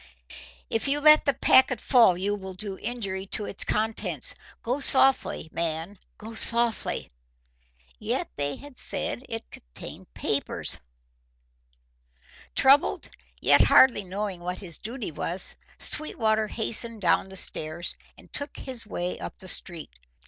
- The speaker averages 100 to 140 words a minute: Yes, slow, 135 wpm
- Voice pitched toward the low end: No, high, 215 Hz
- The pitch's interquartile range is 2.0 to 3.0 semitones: No, average, 4.7 semitones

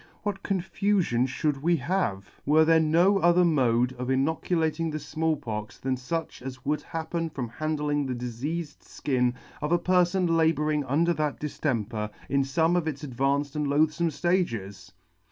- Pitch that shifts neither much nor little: Yes, average, 4.0 semitones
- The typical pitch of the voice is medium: Yes, medium, 150 Hz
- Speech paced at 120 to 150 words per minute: No, average, 160 wpm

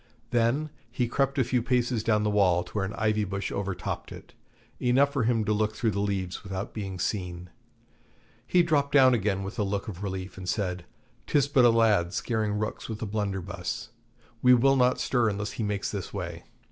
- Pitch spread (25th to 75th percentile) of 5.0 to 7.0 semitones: No, average, 3.9 semitones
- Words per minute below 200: No, fast, 205 wpm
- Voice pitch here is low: Yes, low, 105 Hz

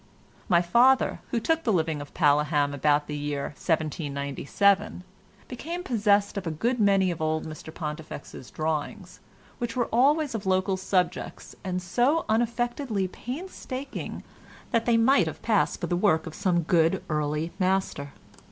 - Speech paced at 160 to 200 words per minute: No, average, 150 wpm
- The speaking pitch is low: No, medium, 185 Hz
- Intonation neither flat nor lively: No, wide, 6.8 semitones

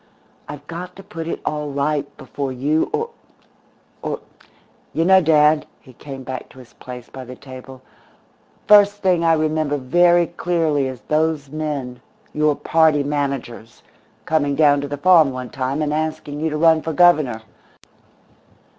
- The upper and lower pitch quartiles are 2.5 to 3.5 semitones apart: Yes, average, 3.0 semitones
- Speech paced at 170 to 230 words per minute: No, average, 160 wpm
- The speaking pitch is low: No, medium, 150 Hz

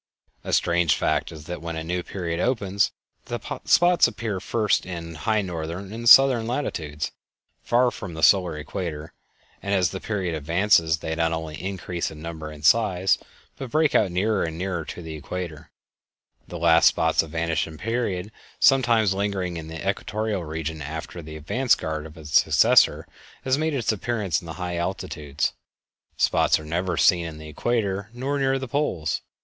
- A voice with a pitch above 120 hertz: No, very low, 90 Hz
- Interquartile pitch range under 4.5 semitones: No, average, 5.0 semitones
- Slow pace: No, average, 175 wpm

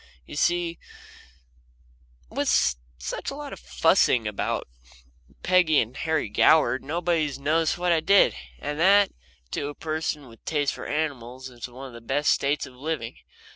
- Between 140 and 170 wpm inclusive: Yes, average, 165 wpm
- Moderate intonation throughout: Yes, average, 4.3 semitones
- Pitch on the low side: No, medium, 150 Hz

